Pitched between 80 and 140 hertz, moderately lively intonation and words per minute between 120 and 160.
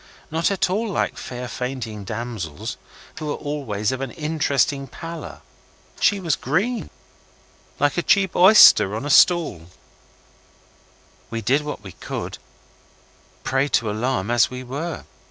No: low, 135 Hz; wide, 5.9 semitones; average, 140 wpm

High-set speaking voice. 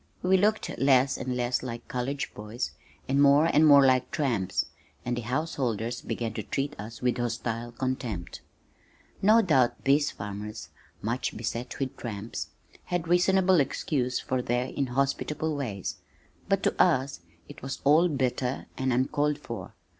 No: low, 130 Hz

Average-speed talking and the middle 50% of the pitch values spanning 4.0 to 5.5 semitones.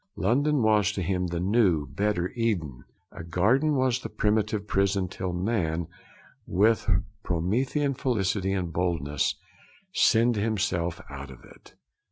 No: slow, 130 wpm; average, 4.6 semitones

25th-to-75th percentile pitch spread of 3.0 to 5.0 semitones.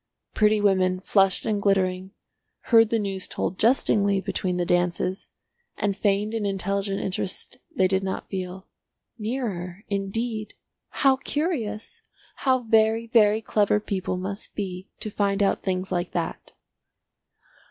No: narrow, 2.4 semitones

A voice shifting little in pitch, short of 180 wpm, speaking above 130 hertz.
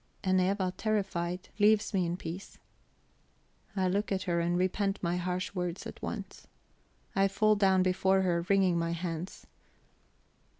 Yes: narrow, 1.9 semitones; average, 145 wpm; medium, 185 Hz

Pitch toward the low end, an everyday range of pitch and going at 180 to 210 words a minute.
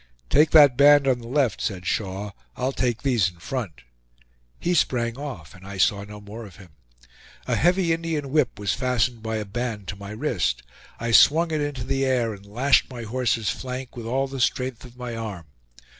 Yes: low, 120 Hz; average, 4.5 semitones; average, 200 wpm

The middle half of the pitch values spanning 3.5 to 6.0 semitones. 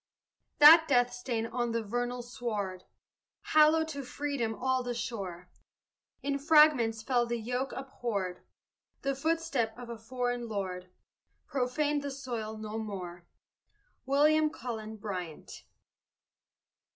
Yes: average, 4.0 semitones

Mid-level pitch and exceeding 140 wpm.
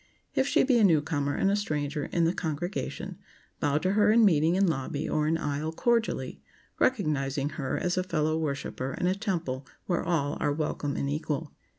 Yes: medium, 160 Hz; average, 190 wpm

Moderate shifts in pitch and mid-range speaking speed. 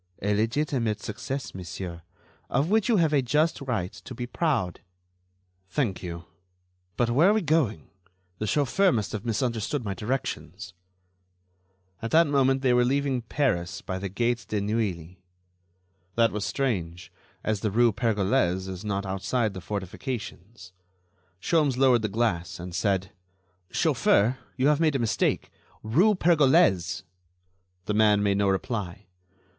No: wide, 5.7 semitones; average, 145 wpm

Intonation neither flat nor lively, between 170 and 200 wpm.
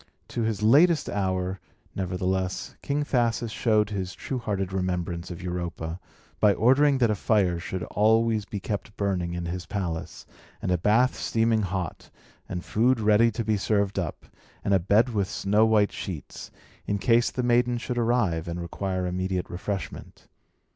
No: average, 3.8 semitones; average, 160 wpm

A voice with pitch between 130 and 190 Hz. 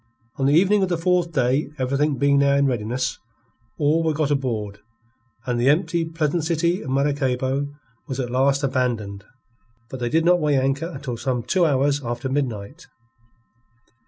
Yes: medium, 140 Hz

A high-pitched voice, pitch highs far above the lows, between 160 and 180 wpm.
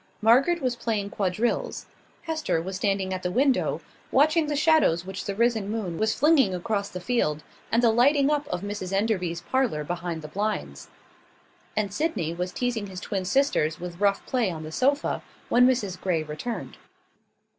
Yes: high, 205 Hz; wide, 5.9 semitones; average, 170 wpm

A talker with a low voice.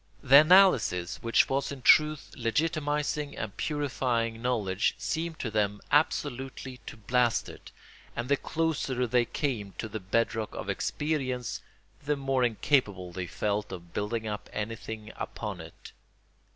Yes: low, 125 Hz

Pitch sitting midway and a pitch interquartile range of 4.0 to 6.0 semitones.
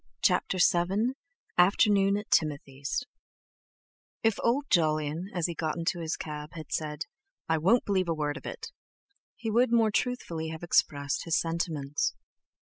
Yes: medium, 170 Hz; average, 4.5 semitones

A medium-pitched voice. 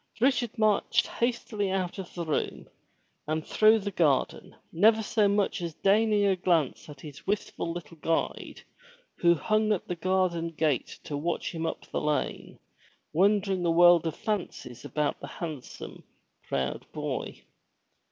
Yes: medium, 175 Hz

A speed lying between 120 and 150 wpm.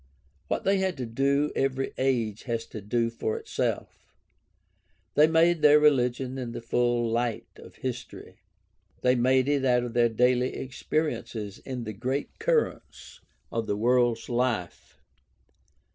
Yes: average, 145 wpm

